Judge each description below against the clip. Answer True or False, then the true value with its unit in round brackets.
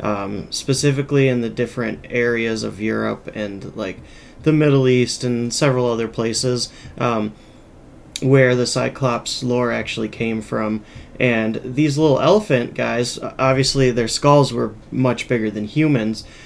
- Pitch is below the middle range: True (120 Hz)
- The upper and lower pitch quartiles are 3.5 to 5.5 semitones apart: False (2.9 semitones)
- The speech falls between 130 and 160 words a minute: True (140 wpm)